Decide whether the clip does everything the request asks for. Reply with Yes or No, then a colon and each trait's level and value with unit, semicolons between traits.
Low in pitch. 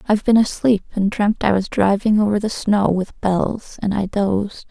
No: high, 205 Hz